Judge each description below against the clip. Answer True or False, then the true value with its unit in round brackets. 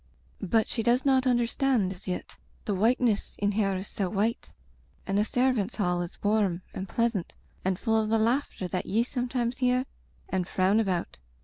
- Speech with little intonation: False (4.1 semitones)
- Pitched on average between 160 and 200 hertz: False (215 Hz)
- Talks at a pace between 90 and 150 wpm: False (190 wpm)